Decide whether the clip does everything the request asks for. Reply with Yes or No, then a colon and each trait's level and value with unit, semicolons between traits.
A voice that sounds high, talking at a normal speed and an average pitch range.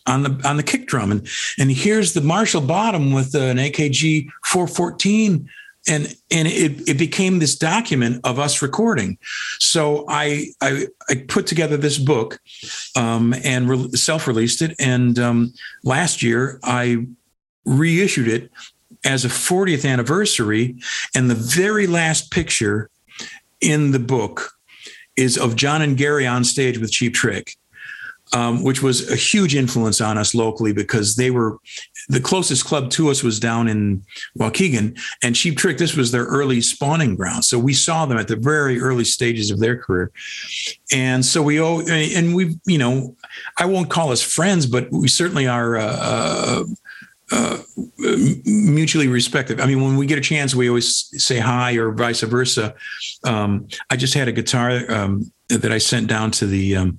No: low, 130 Hz; average, 170 wpm; average, 4.8 semitones